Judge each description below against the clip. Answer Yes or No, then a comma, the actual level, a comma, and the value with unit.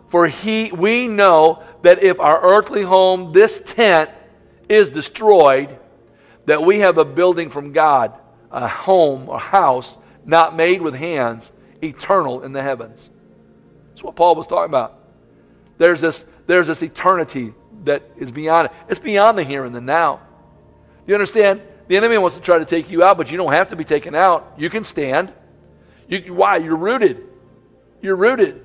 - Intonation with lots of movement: No, average, 5.0 semitones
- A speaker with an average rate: Yes, average, 170 wpm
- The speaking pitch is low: No, medium, 170 Hz